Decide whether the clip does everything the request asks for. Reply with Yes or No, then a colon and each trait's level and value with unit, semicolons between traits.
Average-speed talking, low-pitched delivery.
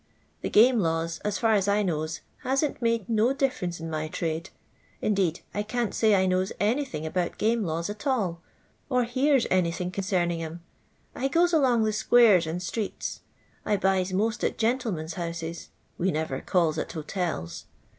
No: average, 165 wpm; high, 190 Hz